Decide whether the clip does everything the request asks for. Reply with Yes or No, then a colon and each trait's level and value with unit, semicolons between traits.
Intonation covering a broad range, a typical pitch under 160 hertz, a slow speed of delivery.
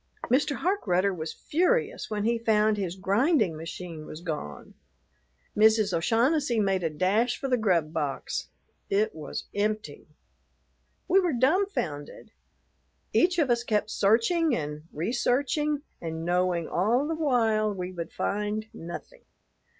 No: wide, 6.9 semitones; high, 215 Hz; slow, 130 wpm